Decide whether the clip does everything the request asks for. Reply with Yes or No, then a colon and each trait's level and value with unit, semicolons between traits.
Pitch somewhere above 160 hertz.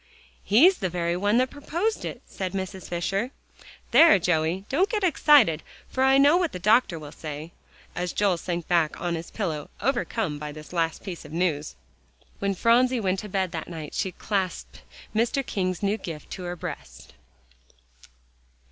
Yes: high, 190 Hz